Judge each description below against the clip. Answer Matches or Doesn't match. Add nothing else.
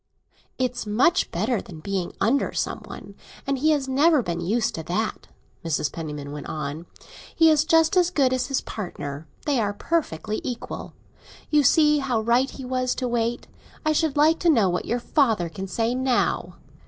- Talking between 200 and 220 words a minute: Doesn't match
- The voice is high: Matches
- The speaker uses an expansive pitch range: Matches